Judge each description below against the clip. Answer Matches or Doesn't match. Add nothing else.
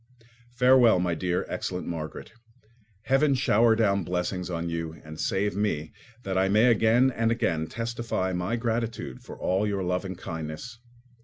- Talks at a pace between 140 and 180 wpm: Matches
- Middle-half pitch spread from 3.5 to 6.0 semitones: Matches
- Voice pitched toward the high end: Doesn't match